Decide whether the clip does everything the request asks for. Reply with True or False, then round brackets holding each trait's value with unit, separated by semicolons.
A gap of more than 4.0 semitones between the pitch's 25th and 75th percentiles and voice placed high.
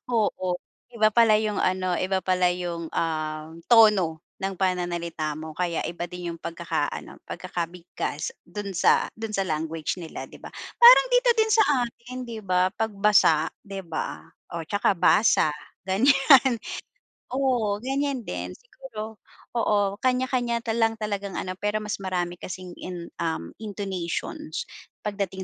True (4.4 semitones; 195 Hz)